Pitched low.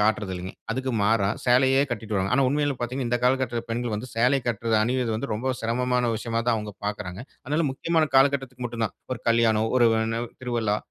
Yes: low, 120 Hz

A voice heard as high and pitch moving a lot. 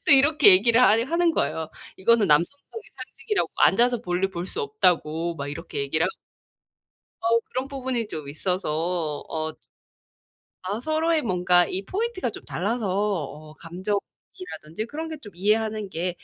Yes: high, 205 Hz; wide, 7.0 semitones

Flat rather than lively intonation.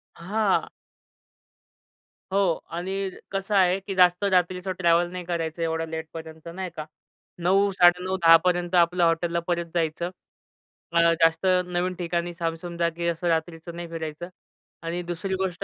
Yes: narrow, 1.6 semitones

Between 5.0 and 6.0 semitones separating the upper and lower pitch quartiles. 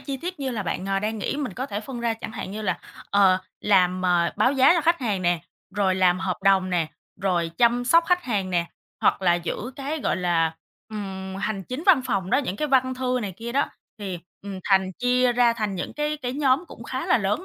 Yes: wide, 5.5 semitones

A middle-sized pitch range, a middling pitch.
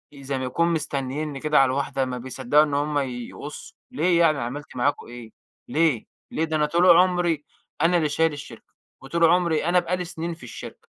Yes: average, 3.7 semitones; medium, 150 Hz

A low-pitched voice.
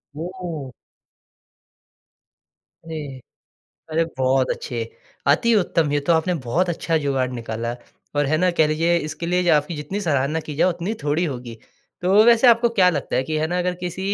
No: medium, 160 Hz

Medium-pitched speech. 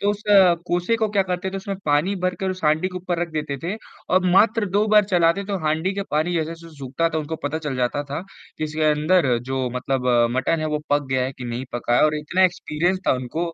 Yes: medium, 165 Hz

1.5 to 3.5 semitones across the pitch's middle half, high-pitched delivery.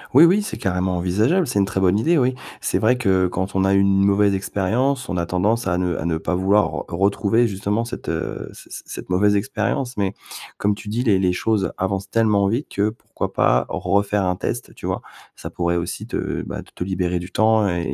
No: average, 3.1 semitones; low, 100 Hz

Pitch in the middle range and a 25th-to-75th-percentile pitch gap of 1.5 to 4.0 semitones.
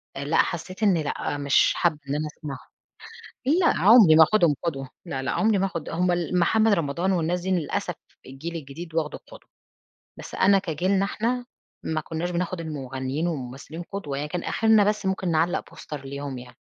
No: medium, 170 Hz; average, 4.6 semitones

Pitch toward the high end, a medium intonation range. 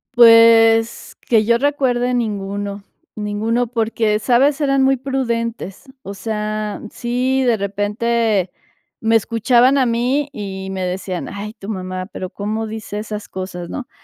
Yes: high, 225 Hz; average, 3.1 semitones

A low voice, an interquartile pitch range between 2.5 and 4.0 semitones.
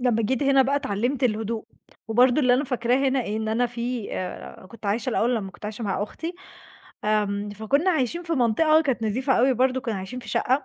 No: high, 245 Hz; average, 3.6 semitones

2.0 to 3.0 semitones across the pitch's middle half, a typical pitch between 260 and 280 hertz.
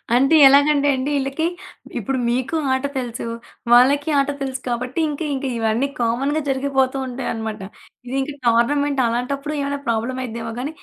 Yes: average, 2.7 semitones; very high, 265 Hz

